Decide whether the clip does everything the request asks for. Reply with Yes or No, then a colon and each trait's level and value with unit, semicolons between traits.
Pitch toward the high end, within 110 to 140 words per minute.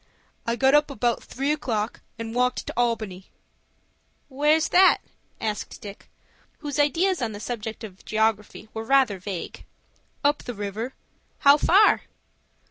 Yes: high, 240 Hz; slow, 135 wpm